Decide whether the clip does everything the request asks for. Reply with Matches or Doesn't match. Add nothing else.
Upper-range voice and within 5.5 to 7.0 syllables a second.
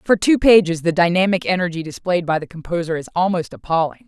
Doesn't match